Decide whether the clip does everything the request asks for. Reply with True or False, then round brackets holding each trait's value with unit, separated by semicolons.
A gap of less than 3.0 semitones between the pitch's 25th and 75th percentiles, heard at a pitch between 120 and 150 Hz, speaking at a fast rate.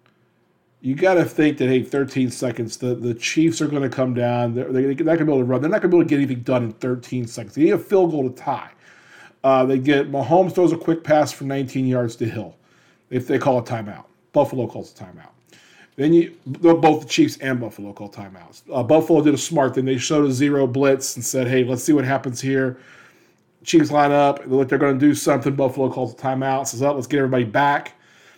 True (2.6 semitones; 135 Hz; 245 wpm)